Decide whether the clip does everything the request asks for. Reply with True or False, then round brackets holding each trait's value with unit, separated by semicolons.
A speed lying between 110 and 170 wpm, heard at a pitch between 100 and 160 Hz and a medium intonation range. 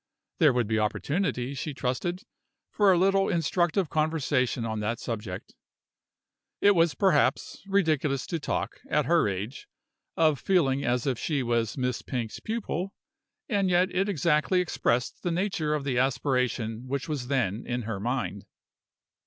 False (150 wpm; 140 Hz; 6.0 semitones)